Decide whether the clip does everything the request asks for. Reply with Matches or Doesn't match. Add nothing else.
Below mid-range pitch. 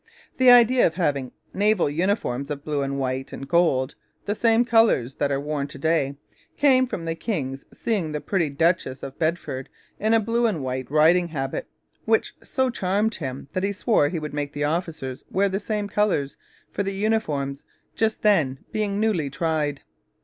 Doesn't match